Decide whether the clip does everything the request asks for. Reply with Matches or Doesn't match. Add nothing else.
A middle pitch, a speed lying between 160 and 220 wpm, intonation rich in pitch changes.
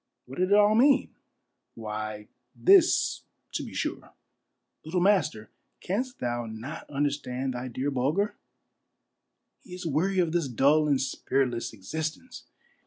Doesn't match